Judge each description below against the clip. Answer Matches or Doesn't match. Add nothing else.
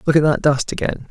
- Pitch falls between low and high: Matches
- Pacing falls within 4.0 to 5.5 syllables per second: Doesn't match